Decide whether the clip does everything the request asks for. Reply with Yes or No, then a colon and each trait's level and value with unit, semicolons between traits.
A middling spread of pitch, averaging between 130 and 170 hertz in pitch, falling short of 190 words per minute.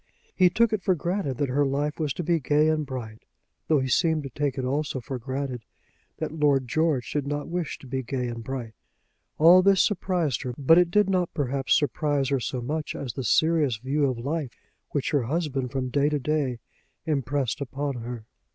No: average, 3.4 semitones; medium, 140 Hz; fast, 205 wpm